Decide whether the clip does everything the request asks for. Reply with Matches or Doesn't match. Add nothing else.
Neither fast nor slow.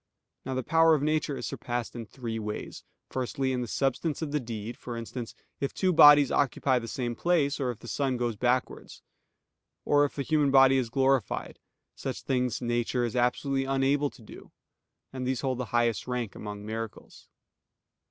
Matches